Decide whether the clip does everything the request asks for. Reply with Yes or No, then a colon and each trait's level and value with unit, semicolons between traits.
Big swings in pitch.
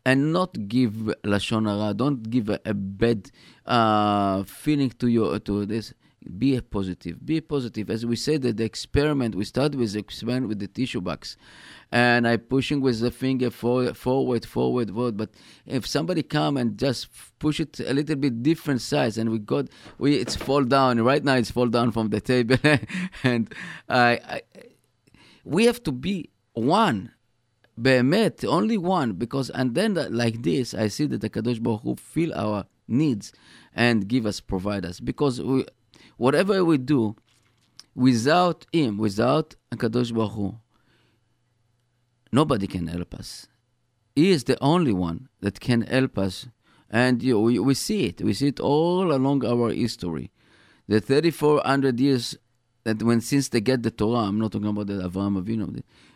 No: average, 3.7 semitones